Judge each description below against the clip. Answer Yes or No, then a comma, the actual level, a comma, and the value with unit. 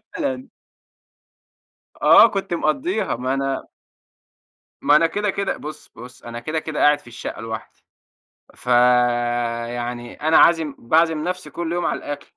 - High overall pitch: No, medium, 145 Hz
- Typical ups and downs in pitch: No, wide, 5.8 semitones